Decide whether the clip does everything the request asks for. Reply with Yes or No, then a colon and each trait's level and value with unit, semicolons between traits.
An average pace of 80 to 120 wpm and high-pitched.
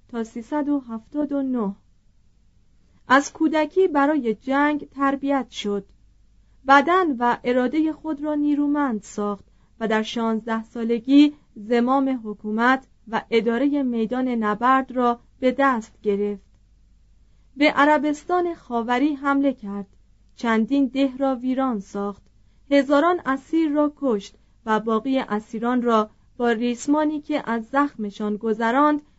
Yes: average, 110 wpm; very high, 250 Hz